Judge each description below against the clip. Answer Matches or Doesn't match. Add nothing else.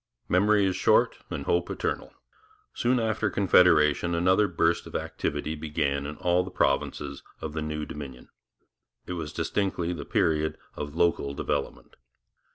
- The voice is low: Matches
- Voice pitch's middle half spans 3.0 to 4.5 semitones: Matches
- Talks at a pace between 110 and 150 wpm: Matches